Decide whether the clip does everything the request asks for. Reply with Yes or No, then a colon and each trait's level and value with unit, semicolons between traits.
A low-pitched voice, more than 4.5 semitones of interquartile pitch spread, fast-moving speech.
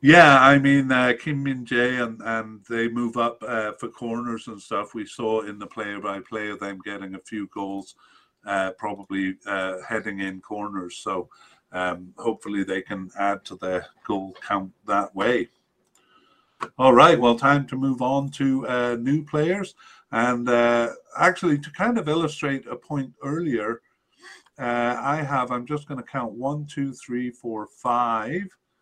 No: low, 120 Hz; average, 5.2 semitones; average, 170 wpm